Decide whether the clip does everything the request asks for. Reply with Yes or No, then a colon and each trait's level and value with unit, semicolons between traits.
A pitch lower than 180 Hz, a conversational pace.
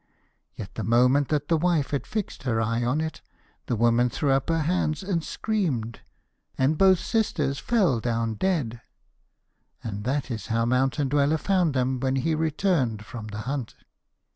Yes: low, 135 Hz; average, 165 wpm